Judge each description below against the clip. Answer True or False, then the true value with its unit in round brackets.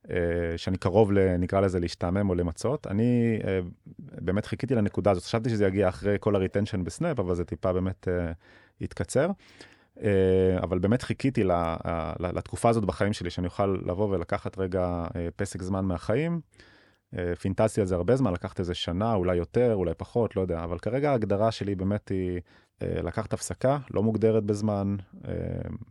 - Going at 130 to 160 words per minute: True (150 wpm)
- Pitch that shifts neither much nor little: True (3.4 semitones)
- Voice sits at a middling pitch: False (95 Hz)